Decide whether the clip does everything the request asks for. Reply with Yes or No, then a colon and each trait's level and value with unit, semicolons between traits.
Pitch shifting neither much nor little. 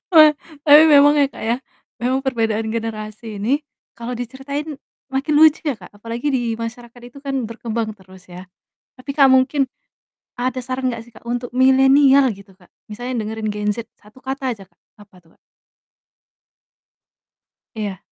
Yes: average, 3.4 semitones